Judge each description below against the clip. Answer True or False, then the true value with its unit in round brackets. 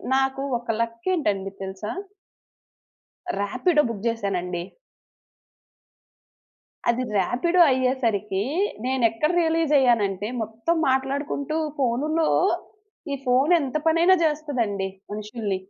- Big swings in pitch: True (5.9 semitones)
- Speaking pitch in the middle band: False (250 Hz)